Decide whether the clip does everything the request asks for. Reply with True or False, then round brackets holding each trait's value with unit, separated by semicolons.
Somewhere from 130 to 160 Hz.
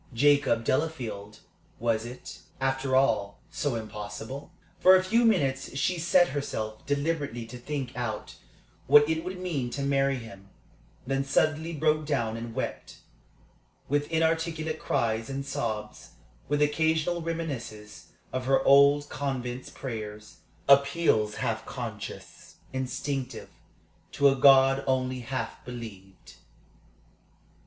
True (135 Hz)